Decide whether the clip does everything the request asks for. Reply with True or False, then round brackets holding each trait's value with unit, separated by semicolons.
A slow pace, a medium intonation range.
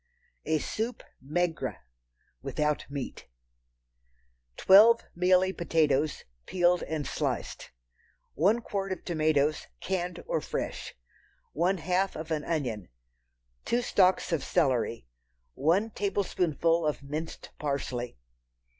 True (100 wpm; 3.9 semitones)